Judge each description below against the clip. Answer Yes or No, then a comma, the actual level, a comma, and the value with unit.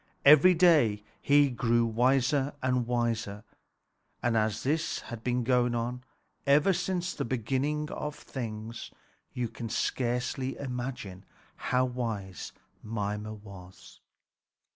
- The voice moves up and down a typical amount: Yes, average, 3.6 semitones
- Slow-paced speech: Yes, slow, 115 wpm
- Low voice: Yes, low, 125 Hz